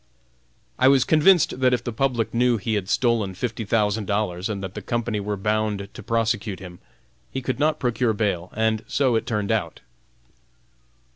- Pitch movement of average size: Yes, average, 3.2 semitones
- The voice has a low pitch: Yes, low, 110 Hz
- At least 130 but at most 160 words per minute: No, average, 180 wpm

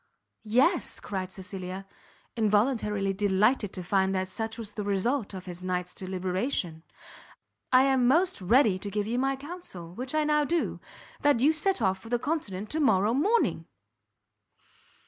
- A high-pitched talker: Yes, high, 210 Hz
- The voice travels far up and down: Yes, wide, 6.2 semitones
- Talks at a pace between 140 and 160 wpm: Yes, average, 155 wpm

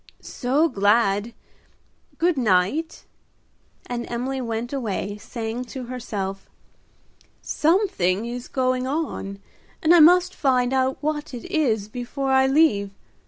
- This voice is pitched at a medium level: No, very high, 250 Hz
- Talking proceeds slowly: Yes, slow, 115 wpm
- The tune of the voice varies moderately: Yes, average, 4.7 semitones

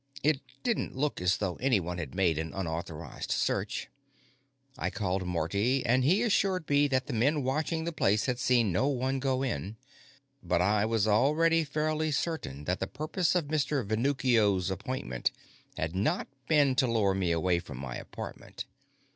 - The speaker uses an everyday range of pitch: No, wide, 7.8 semitones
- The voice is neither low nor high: No, low, 120 Hz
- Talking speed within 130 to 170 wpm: Yes, average, 165 wpm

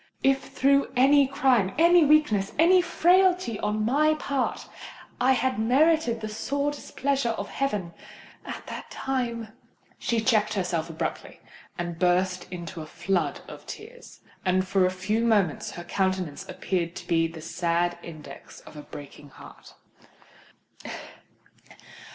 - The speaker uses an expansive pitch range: Yes, wide, 7.7 semitones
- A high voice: Yes, high, 215 Hz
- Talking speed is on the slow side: Yes, slow, 125 wpm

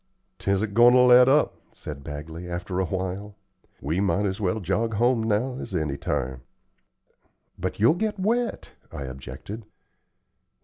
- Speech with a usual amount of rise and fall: No, wide, 5.9 semitones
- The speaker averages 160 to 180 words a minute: No, average, 145 wpm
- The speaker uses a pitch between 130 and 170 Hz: No, low, 100 Hz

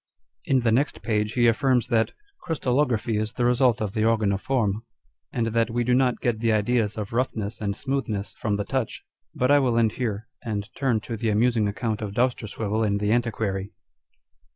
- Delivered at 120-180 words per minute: No, average, 200 wpm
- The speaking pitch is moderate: No, low, 115 Hz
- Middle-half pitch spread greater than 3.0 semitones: No, average, 2.7 semitones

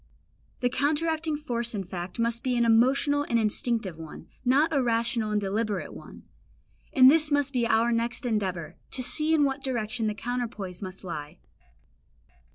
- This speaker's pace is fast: No, average, 165 wpm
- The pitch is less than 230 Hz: No, high, 235 Hz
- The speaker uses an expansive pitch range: No, average, 4.2 semitones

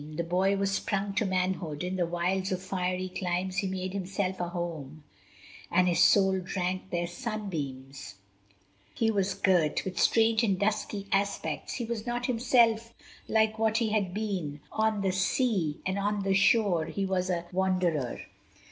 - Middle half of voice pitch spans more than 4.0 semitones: No, average, 2.7 semitones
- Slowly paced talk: No, average, 165 wpm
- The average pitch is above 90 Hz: Yes, high, 190 Hz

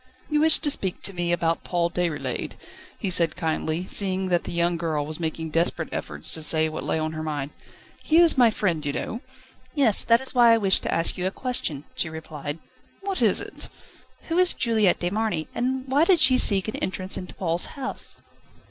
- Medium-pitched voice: Yes, medium, 180 Hz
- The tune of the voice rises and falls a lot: Yes, wide, 6.5 semitones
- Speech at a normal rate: No, fast, 210 wpm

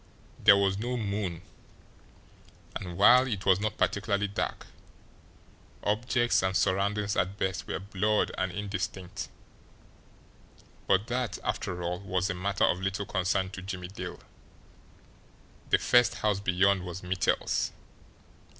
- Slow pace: Yes, slow, 125 wpm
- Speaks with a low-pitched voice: Yes, low, 100 Hz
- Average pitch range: No, narrow, 1.9 semitones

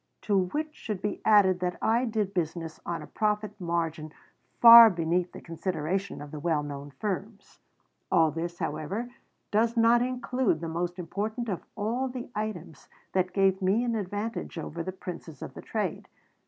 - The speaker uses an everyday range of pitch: Yes, average, 4.7 semitones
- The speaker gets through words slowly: No, average, 170 wpm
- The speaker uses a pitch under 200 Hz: Yes, high, 190 Hz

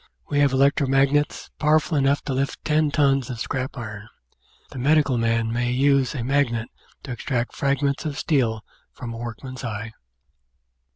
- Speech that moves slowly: No, average, 165 wpm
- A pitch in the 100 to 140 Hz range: Yes, low, 135 Hz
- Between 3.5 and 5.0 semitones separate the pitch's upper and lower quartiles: No, average, 3.1 semitones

